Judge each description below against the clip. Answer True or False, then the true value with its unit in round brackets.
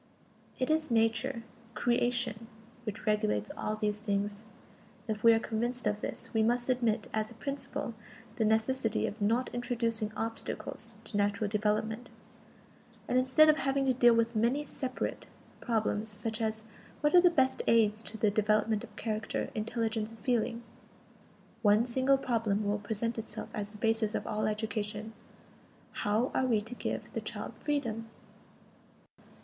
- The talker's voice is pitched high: True (225 Hz)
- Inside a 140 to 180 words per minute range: True (155 wpm)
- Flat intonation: True (2.2 semitones)